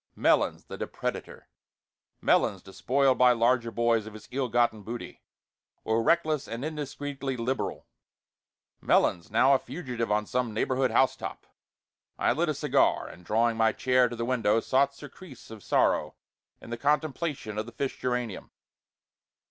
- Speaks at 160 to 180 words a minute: No, average, 150 wpm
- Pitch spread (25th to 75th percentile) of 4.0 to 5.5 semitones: No, average, 3.1 semitones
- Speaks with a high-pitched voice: No, low, 125 Hz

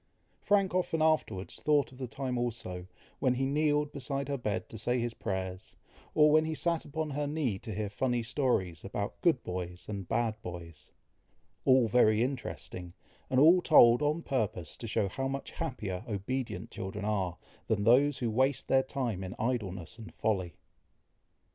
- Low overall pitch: Yes, low, 120 Hz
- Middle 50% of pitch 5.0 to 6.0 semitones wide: Yes, wide, 5.6 semitones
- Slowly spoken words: No, average, 170 wpm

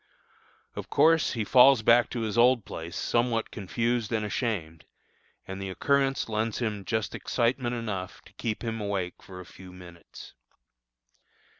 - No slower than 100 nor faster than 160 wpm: Yes, average, 150 wpm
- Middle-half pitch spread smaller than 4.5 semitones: Yes, average, 3.9 semitones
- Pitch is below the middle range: Yes, low, 110 Hz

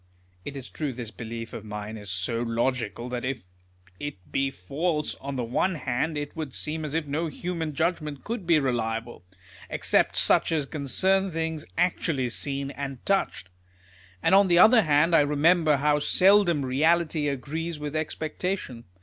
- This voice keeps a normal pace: Yes, average, 165 wpm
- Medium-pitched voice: Yes, medium, 145 Hz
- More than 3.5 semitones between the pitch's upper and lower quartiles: Yes, average, 4.6 semitones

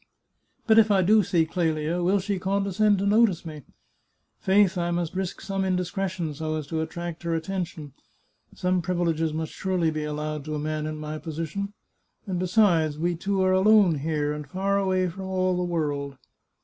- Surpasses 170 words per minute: Yes, average, 180 wpm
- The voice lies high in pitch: No, medium, 175 Hz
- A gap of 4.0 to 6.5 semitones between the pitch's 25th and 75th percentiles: No, average, 3.4 semitones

